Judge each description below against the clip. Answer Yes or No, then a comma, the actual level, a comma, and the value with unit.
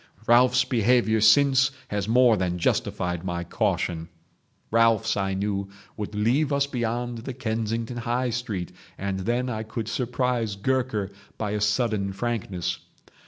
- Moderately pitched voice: No, low, 115 Hz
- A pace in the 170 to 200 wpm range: No, slow, 135 wpm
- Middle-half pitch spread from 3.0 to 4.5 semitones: Yes, average, 3.4 semitones